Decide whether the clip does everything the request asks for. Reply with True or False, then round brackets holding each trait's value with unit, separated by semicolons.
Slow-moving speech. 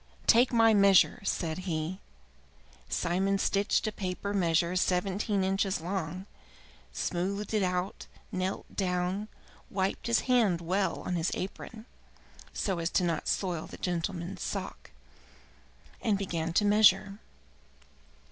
True (120 wpm)